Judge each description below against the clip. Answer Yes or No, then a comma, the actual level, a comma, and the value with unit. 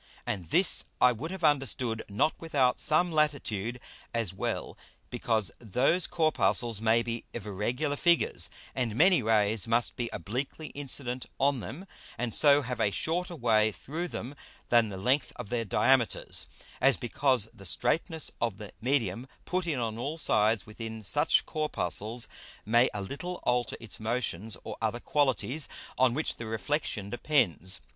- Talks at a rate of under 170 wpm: Yes, average, 155 wpm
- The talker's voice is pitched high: No, low, 120 Hz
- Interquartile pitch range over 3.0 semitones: Yes, average, 4.7 semitones